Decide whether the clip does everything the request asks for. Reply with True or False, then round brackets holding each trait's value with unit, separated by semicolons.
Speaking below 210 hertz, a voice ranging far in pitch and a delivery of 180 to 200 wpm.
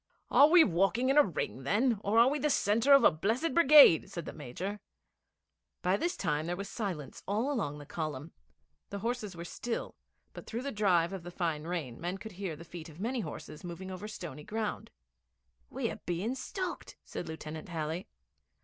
True (190 Hz; 5.9 semitones; 190 wpm)